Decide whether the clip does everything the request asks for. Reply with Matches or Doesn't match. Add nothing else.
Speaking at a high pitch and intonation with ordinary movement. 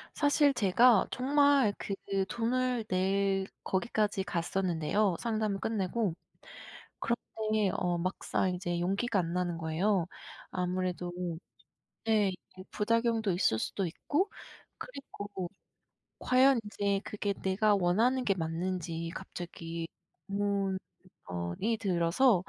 Matches